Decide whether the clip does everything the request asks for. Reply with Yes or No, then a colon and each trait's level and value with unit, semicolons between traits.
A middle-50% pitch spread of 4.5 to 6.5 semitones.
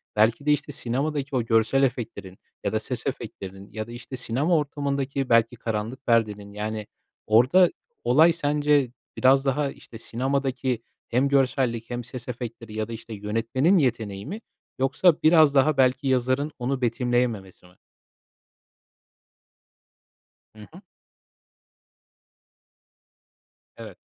No: average, 3.6 semitones